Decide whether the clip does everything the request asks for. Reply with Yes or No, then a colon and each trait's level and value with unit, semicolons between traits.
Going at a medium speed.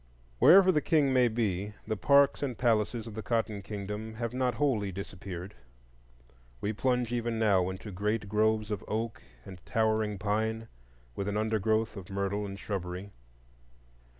Yes: average, 150 wpm